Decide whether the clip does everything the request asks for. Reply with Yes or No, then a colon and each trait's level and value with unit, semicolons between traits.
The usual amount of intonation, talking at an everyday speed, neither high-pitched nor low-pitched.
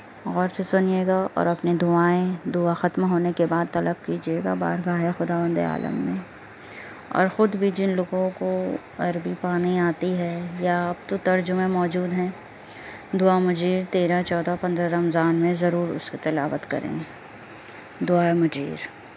No: narrow, 1.4 semitones; average, 145 wpm; medium, 175 Hz